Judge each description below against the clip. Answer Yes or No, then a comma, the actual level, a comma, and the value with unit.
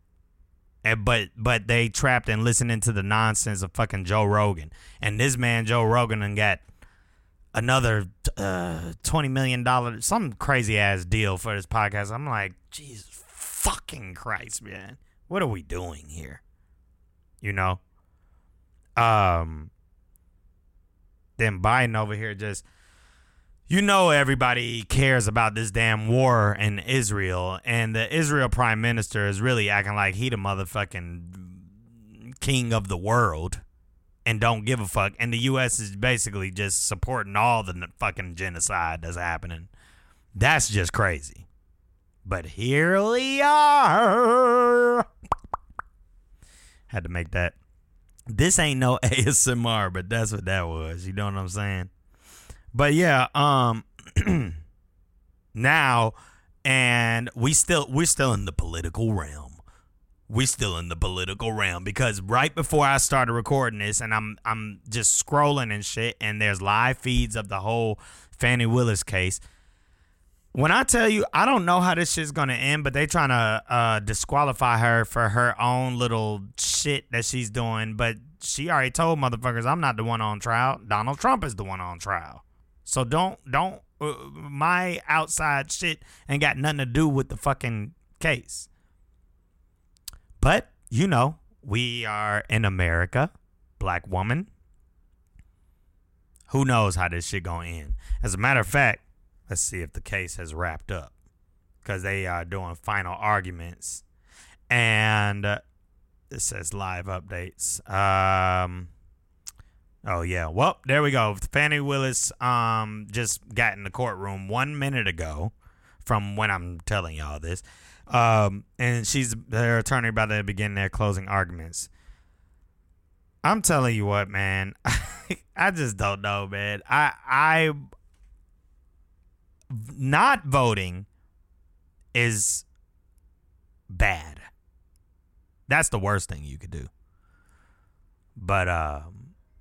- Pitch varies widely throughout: Yes, wide, 5.9 semitones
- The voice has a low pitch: Yes, low, 105 Hz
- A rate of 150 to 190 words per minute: No, average, 140 wpm